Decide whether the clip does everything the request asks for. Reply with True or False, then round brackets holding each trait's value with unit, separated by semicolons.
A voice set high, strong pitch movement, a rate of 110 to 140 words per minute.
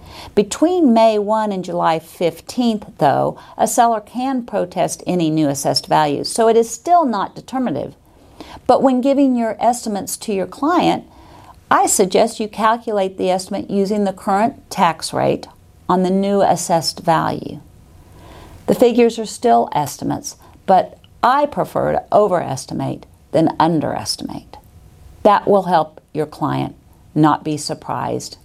True (205 Hz; 5.8 semitones; 135 wpm)